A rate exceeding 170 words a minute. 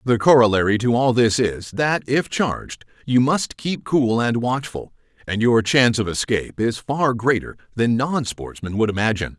Yes: average, 180 wpm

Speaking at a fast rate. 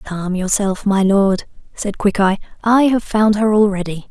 No: average, 160 wpm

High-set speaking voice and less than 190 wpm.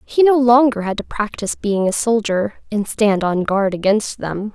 No: high, 215 Hz; average, 200 wpm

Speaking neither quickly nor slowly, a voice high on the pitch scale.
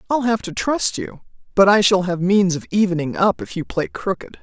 No: fast, 230 wpm; high, 195 Hz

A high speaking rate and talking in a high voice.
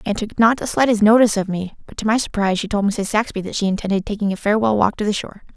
Yes: fast, 280 wpm; high, 210 Hz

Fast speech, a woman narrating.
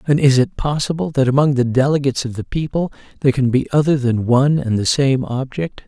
No: fast, 215 wpm; male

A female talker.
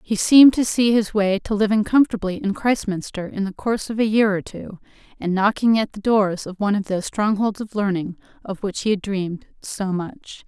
Yes: female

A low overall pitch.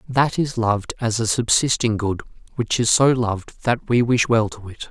Yes: low, 115 Hz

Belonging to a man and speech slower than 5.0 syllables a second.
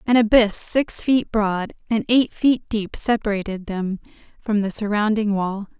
No: female; 4.5 syllables/s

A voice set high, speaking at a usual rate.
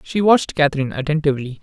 No: medium, 150 Hz; average, 145 wpm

